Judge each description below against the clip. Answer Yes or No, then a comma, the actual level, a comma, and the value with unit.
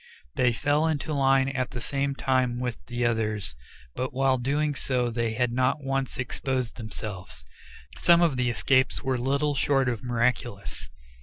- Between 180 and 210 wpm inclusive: No, average, 160 wpm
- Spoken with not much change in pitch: Yes, narrow, 2.2 semitones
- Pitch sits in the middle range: No, low, 130 Hz